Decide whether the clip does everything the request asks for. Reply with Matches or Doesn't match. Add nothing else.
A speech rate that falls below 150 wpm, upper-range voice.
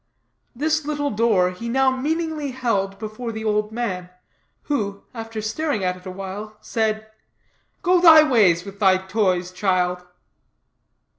Matches